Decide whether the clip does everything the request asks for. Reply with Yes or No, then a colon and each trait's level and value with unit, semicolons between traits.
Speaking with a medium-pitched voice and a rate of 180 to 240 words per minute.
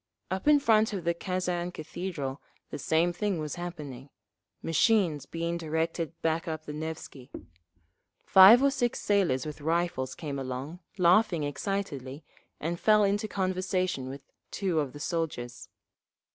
No: medium, 170 Hz; average, 140 wpm